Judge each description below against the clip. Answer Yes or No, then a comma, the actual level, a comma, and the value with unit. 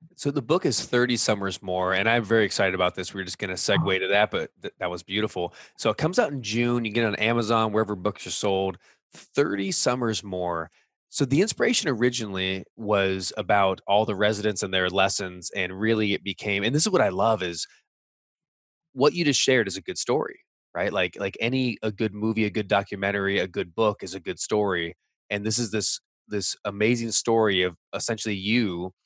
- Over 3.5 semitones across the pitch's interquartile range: No, average, 3.2 semitones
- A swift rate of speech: Yes, fast, 215 wpm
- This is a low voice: Yes, low, 105 Hz